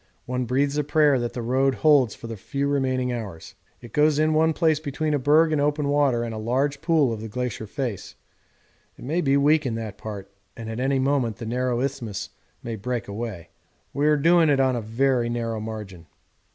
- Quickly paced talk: Yes, fast, 210 wpm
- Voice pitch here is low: Yes, low, 130 Hz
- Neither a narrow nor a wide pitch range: Yes, average, 4.1 semitones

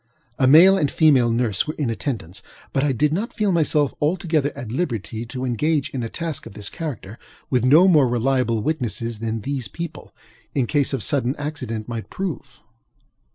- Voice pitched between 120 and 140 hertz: Yes, low, 135 Hz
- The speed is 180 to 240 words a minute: Yes, average, 185 wpm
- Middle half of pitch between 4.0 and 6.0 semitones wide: Yes, average, 4.8 semitones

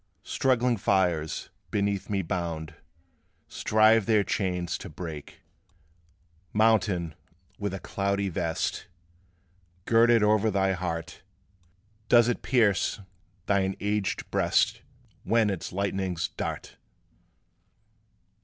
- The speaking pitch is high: No, low, 100 Hz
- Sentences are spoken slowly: Yes, slow, 95 wpm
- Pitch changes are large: No, average, 3.3 semitones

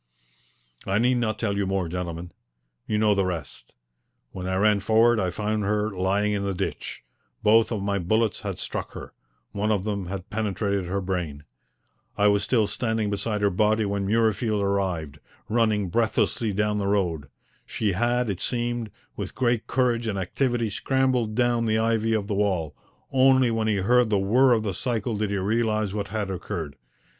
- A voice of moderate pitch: No, low, 105 Hz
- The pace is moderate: Yes, average, 180 wpm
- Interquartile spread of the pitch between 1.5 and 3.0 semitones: Yes, narrow, 2.6 semitones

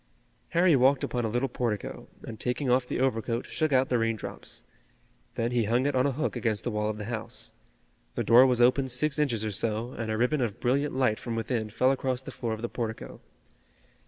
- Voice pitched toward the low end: Yes, low, 120 Hz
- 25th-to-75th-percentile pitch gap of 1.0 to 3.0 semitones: Yes, average, 2.7 semitones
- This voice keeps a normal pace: No, fast, 220 wpm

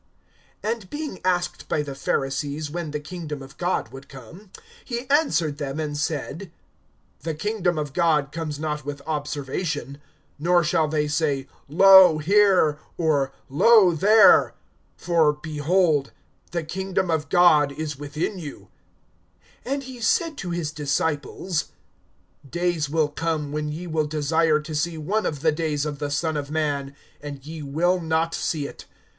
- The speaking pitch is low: No, medium, 155 Hz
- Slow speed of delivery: No, average, 150 wpm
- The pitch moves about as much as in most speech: Yes, average, 3.1 semitones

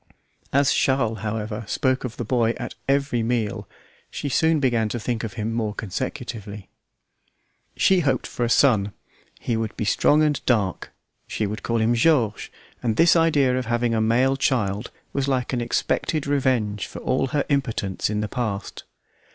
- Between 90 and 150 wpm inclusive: No, average, 170 wpm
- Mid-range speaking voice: No, low, 120 Hz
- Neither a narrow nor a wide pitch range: Yes, average, 3.6 semitones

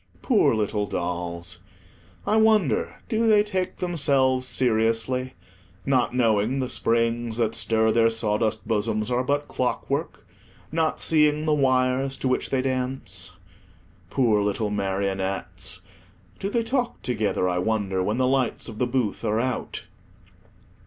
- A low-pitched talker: Yes, low, 120 Hz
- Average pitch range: Yes, average, 4.3 semitones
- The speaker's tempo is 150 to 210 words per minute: No, slow, 135 wpm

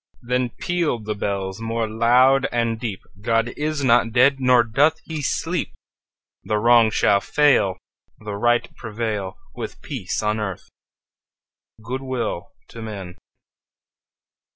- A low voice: Yes, low, 115 Hz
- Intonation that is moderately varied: Yes, average, 3.3 semitones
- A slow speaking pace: Yes, slow, 130 wpm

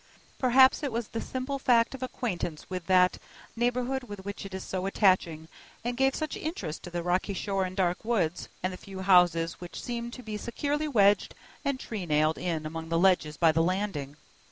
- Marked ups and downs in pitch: Yes, wide, 5.7 semitones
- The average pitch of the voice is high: Yes, high, 195 Hz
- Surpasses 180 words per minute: Yes, average, 195 wpm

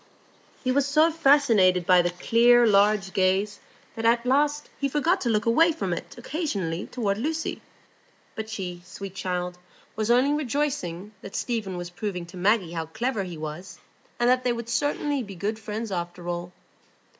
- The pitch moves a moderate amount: No, wide, 6.0 semitones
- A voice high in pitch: Yes, high, 215 Hz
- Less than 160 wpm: No, average, 170 wpm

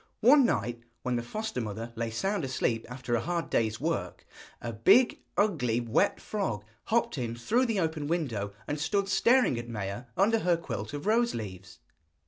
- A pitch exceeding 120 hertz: Yes, low, 135 Hz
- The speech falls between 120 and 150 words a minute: No, average, 175 wpm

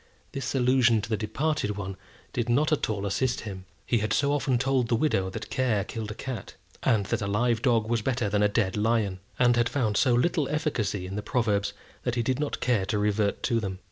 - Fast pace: Yes, fast, 230 wpm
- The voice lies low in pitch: Yes, low, 115 Hz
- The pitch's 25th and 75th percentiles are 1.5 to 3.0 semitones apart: No, average, 3.4 semitones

